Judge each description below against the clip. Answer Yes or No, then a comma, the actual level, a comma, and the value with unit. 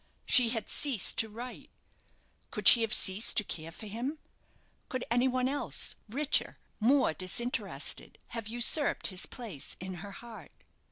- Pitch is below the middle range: No, high, 230 Hz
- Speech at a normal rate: Yes, average, 150 wpm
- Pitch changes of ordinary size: Yes, average, 3.8 semitones